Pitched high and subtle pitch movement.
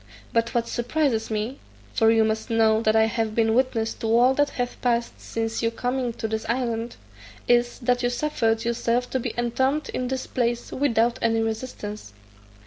Yes: high, 235 Hz; narrow, 1.7 semitones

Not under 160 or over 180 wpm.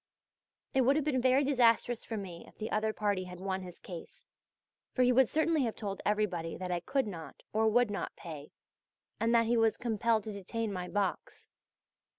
No: average, 195 wpm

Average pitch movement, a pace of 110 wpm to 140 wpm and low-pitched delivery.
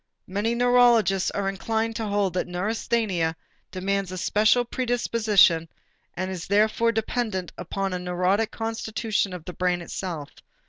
No: average, 3.6 semitones; slow, 135 wpm; high, 200 Hz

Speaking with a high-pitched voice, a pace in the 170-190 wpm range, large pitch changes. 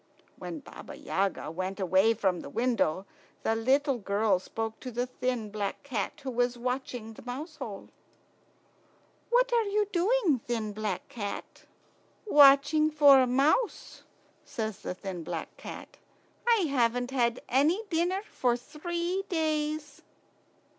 No: very high, 250 Hz; slow, 135 wpm; wide, 5.9 semitones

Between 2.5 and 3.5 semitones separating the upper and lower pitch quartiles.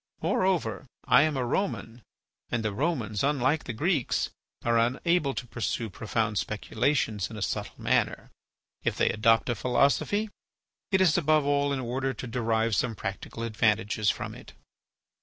No: average, 4.4 semitones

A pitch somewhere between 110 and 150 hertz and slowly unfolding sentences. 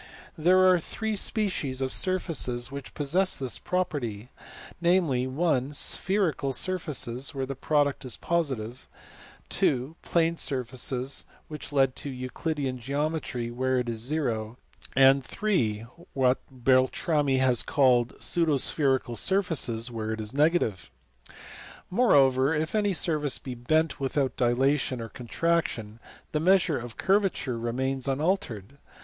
Yes: low, 135 Hz; slow, 125 wpm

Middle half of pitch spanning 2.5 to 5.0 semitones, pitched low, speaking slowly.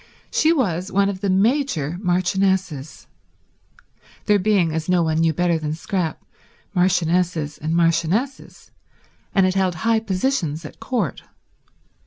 No: average, 3.5 semitones; medium, 180 Hz; slow, 120 wpm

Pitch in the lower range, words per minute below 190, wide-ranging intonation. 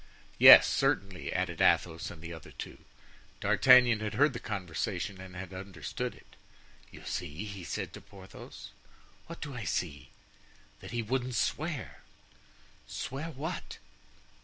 Yes: low, 100 Hz; slow, 135 wpm; wide, 5.8 semitones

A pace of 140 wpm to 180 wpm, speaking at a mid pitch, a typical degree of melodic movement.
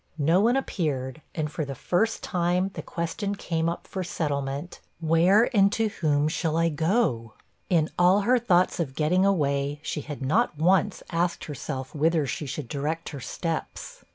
Yes: average, 170 wpm; medium, 165 Hz; average, 4.1 semitones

